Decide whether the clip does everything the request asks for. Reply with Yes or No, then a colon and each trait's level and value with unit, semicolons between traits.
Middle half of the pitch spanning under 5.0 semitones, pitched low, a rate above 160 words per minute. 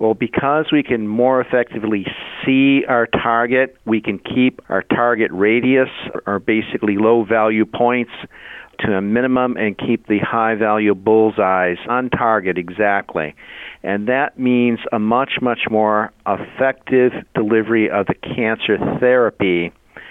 No: average, 2.9 semitones; low, 115 Hz; slow, 135 wpm